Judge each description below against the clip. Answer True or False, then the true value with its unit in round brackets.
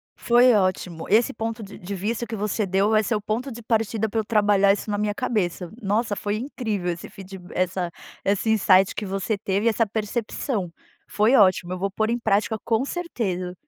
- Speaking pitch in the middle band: False (210 Hz)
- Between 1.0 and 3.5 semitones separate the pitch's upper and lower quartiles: True (2.7 semitones)